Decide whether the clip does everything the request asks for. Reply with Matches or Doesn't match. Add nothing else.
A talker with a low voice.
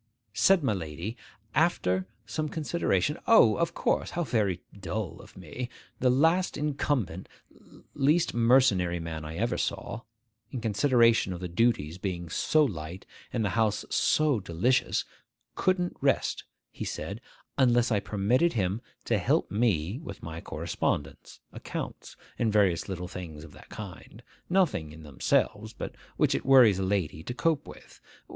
Matches